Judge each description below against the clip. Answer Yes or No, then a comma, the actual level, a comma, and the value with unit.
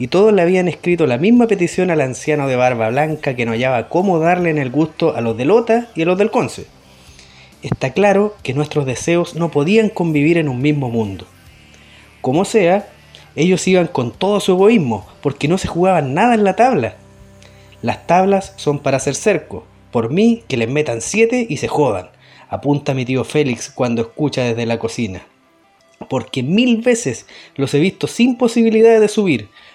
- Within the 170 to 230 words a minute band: Yes, average, 185 wpm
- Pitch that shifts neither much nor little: No, wide, 7.7 semitones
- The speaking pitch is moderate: Yes, medium, 150 Hz